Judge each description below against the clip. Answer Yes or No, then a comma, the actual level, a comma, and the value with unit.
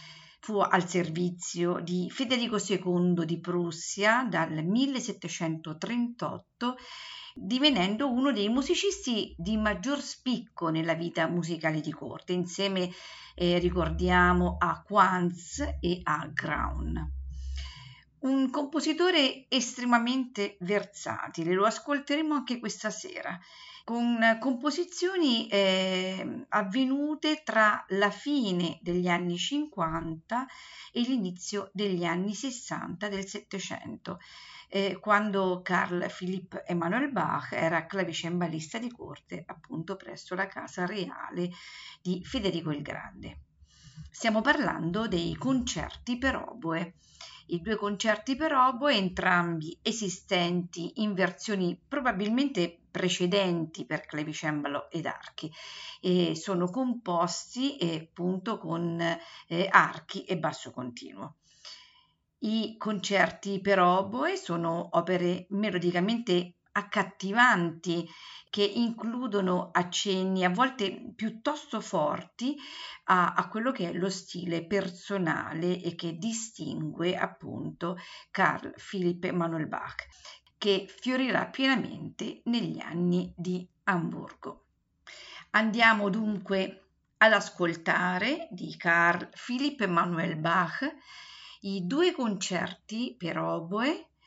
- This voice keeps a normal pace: No, slow, 100 wpm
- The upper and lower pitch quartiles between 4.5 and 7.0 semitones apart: Yes, wide, 5.4 semitones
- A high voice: Yes, high, 195 Hz